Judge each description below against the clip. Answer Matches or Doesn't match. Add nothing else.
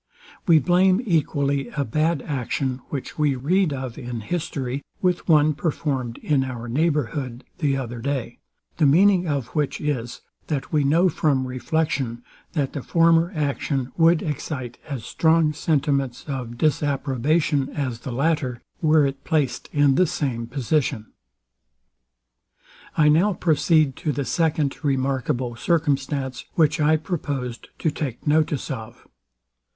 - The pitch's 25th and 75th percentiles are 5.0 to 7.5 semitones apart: Doesn't match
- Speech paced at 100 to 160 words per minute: Matches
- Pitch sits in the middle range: Matches